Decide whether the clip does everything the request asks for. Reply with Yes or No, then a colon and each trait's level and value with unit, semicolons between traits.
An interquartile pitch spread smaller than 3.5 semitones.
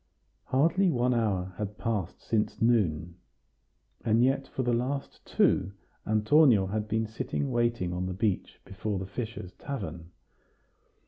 No: average, 4.5 semitones